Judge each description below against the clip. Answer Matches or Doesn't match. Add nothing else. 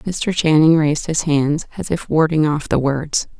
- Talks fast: Doesn't match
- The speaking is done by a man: Doesn't match